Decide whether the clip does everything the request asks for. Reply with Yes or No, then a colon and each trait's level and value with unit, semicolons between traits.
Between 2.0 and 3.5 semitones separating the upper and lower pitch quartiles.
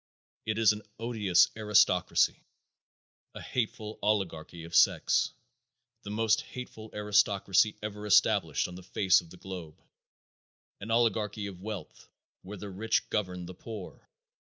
Yes: average, 2.8 semitones